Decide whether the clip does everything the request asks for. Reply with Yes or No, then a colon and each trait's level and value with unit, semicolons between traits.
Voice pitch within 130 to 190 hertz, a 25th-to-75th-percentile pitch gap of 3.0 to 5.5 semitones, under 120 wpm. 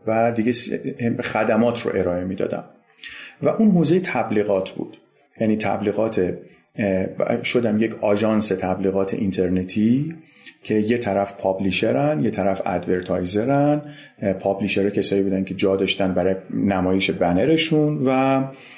No: low, 105 Hz; average, 4.7 semitones; average, 110 wpm